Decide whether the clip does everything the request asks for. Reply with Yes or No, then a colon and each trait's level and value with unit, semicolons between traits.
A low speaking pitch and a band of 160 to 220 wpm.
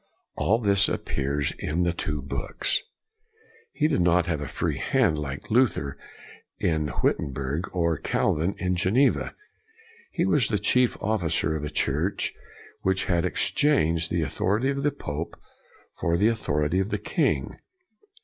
No: very low, 85 Hz; average, 150 wpm